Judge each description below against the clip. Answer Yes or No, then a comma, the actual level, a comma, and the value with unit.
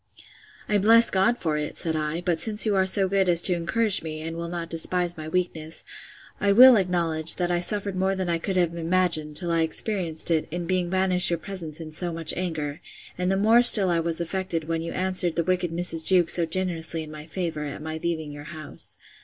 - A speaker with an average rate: No, fast, 225 wpm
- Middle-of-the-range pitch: Yes, medium, 175 Hz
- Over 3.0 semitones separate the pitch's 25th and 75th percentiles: No, narrow, 2.6 semitones